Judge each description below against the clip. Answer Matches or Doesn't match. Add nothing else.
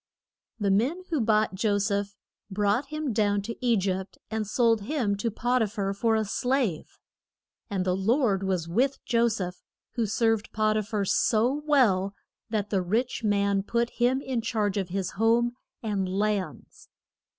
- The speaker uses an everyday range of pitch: Matches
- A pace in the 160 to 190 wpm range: Matches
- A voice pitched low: Doesn't match